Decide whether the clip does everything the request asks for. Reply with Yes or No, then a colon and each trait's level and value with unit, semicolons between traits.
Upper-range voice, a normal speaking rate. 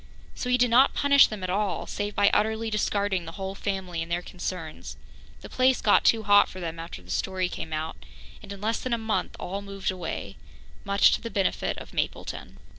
No: high, 200 Hz; fast, 210 wpm